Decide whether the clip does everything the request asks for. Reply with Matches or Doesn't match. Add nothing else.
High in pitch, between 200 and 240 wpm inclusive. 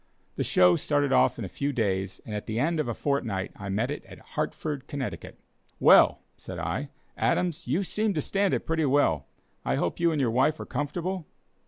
Doesn't match